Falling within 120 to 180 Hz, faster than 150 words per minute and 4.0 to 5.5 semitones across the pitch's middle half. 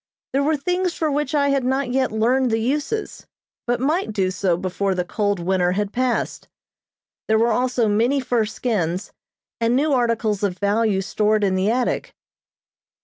No: high, 230 Hz; average, 170 wpm; average, 4.7 semitones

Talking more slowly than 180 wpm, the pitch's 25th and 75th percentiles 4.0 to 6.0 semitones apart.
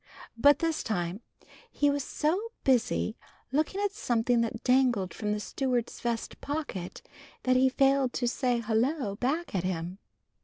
Yes: average, 150 wpm; average, 4.4 semitones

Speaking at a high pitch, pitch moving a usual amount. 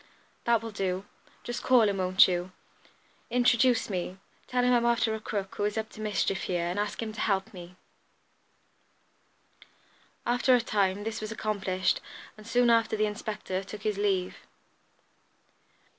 Yes: high, 210 Hz; average, 3.2 semitones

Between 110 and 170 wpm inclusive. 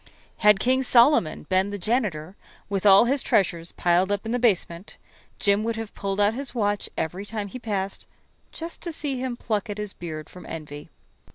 No: average, 190 wpm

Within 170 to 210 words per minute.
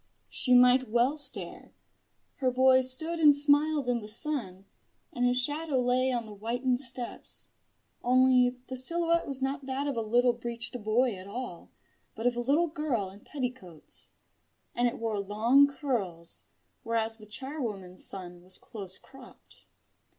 No: average, 155 wpm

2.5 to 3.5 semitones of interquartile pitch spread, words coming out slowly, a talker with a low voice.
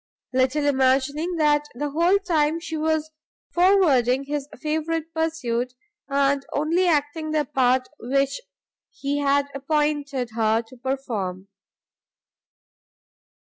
No: average, 3.2 semitones; slow, 105 wpm; very high, 285 Hz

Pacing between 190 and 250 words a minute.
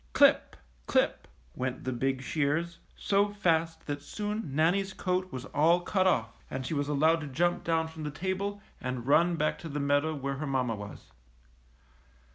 No: average, 175 wpm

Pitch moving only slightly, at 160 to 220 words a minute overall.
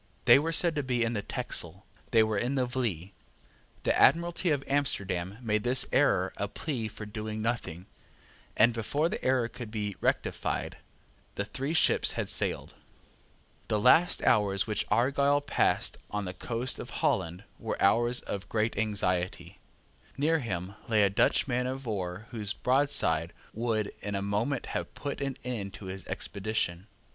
No: average, 4.6 semitones; average, 165 wpm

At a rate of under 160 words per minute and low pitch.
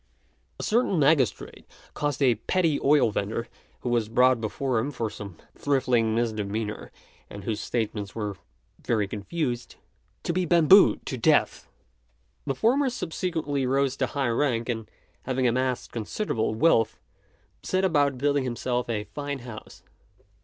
Yes: average, 140 wpm; low, 125 Hz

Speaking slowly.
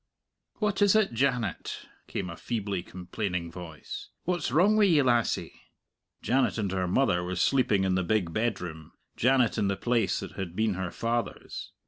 No: average, 165 wpm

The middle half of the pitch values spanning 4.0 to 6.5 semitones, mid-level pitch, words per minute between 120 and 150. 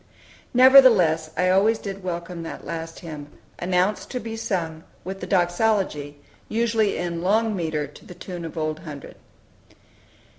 Yes: average, 4.4 semitones; medium, 180 Hz; average, 145 wpm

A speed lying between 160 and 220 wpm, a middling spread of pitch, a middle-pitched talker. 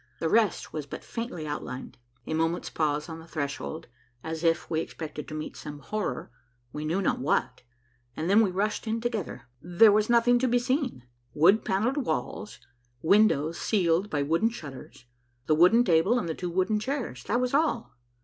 No: average, 180 wpm; wide, 6.4 semitones; medium, 175 Hz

